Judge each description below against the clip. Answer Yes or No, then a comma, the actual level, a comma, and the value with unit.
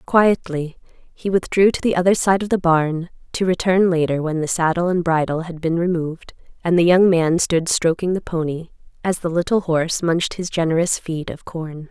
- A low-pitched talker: No, medium, 170 Hz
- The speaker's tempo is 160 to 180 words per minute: No, average, 195 wpm